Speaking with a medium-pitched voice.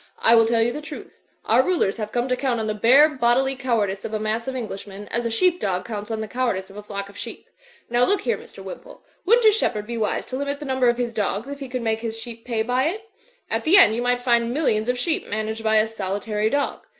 No: high, 235 Hz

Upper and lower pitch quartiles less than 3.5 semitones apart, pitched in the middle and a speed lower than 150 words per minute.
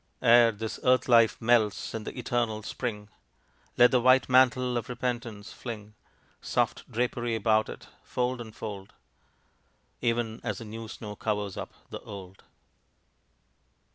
No: narrow, 2.4 semitones; low, 115 Hz; average, 140 wpm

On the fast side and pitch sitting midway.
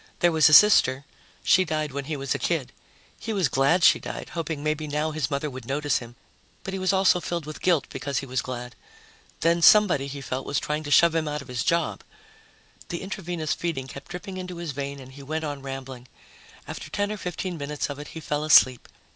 Yes: fast, 220 wpm; medium, 150 Hz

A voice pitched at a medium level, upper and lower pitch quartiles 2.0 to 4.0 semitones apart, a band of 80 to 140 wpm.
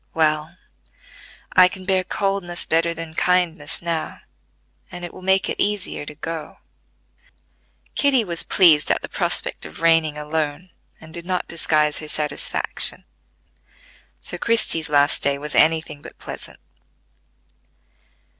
Yes: medium, 165 Hz; average, 3.1 semitones; slow, 135 wpm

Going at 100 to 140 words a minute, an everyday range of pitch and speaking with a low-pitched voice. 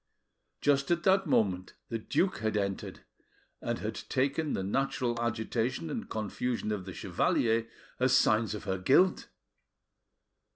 Yes: slow, 135 wpm; average, 4.5 semitones; low, 115 Hz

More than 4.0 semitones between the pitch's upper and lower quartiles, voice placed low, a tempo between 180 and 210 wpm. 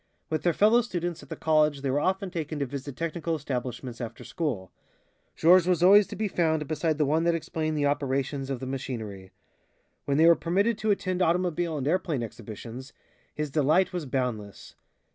No: average, 4.6 semitones; medium, 155 Hz; average, 185 wpm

